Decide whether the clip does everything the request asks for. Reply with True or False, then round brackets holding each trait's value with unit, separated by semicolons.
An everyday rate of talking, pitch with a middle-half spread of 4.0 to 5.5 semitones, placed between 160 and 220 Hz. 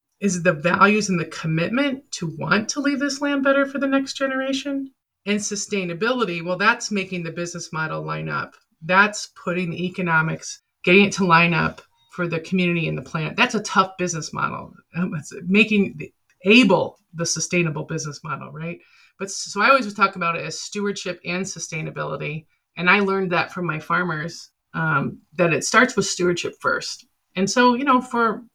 True (185 wpm; 4.8 semitones; 190 Hz)